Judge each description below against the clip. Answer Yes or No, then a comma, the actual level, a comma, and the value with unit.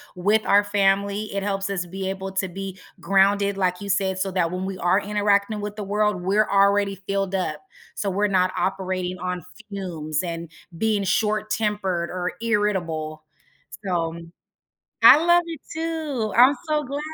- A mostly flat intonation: Yes, narrow, 2.1 semitones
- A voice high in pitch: Yes, high, 195 Hz